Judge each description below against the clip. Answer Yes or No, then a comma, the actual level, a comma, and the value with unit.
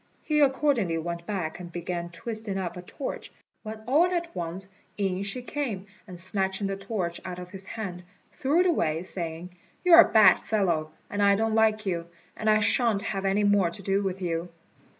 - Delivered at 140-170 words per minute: No, average, 190 wpm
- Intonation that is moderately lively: Yes, average, 3.7 semitones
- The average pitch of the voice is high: Yes, high, 195 Hz